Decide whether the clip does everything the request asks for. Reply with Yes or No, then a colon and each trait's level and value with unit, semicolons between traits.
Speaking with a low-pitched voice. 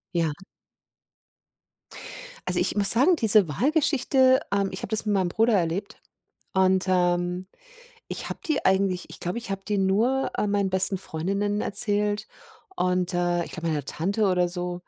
No: high, 190 Hz